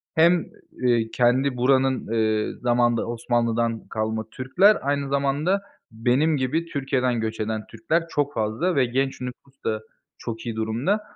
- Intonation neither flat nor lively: Yes, average, 3.7 semitones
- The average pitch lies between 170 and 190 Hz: No, low, 125 Hz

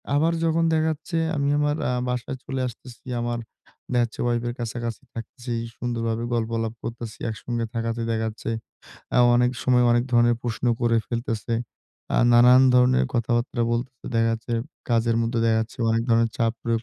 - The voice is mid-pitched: No, low, 120 Hz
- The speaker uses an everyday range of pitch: No, narrow, 1.3 semitones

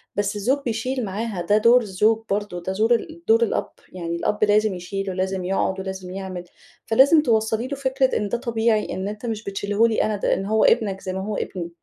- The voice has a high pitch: Yes, high, 210 Hz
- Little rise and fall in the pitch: No, average, 3.2 semitones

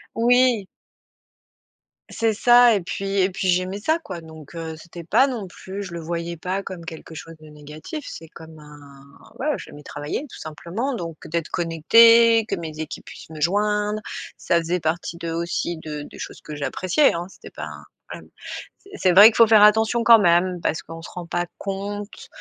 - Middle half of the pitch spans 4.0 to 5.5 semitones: Yes, average, 4.5 semitones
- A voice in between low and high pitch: Yes, medium, 180 Hz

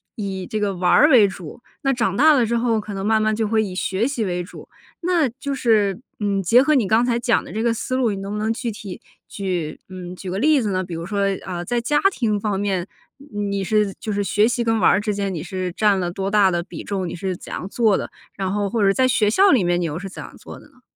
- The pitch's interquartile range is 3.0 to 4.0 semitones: Yes, average, 3.6 semitones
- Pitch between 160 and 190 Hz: No, high, 205 Hz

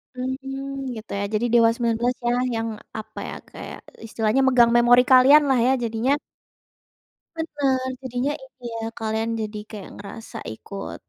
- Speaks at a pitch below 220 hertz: No, high, 245 Hz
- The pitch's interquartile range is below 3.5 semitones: Yes, average, 2.9 semitones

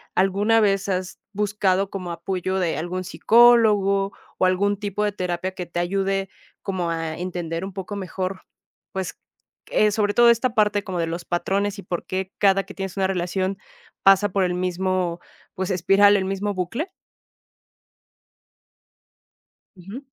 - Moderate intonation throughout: No, narrow, 1.8 semitones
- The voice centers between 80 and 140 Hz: No, high, 190 Hz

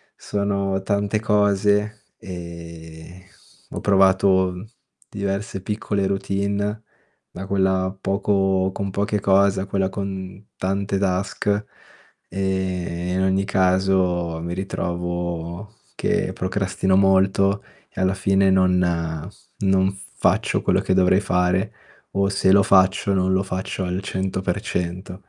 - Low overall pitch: Yes, very low, 95 Hz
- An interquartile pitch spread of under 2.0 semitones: Yes, narrow, 1.2 semitones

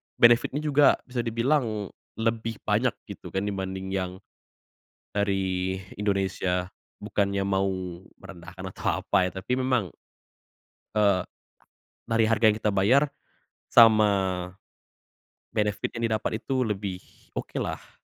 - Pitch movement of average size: Yes, average, 3.3 semitones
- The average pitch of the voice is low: Yes, low, 105 Hz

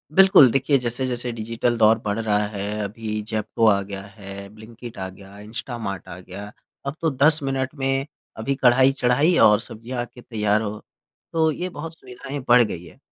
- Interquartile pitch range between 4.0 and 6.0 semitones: Yes, average, 4.3 semitones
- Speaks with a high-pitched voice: No, low, 115 Hz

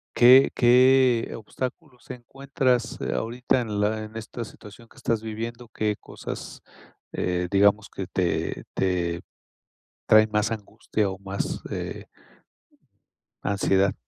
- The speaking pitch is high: No, low, 110 Hz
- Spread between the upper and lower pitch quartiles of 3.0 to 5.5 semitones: Yes, average, 3.3 semitones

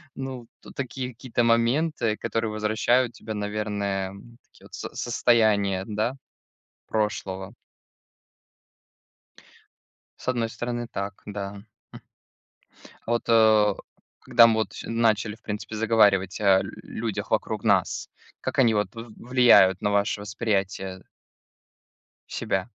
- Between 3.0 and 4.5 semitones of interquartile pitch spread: No, narrow, 2.4 semitones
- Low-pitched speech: Yes, low, 110 Hz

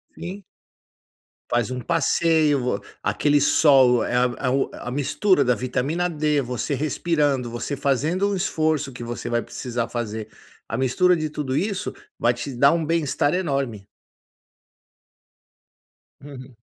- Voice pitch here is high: No, medium, 140 Hz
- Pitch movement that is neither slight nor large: Yes, average, 4.3 semitones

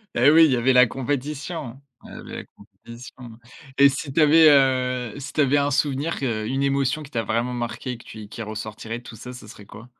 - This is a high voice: No, low, 130 Hz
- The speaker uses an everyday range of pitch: Yes, average, 3.1 semitones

